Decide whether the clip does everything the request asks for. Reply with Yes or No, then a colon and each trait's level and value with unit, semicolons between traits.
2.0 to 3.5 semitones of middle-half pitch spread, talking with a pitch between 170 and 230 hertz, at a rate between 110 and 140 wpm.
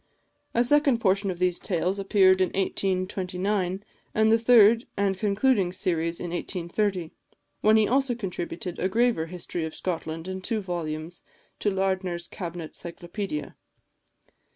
Yes: average, 3.1 semitones; high, 190 Hz; slow, 135 wpm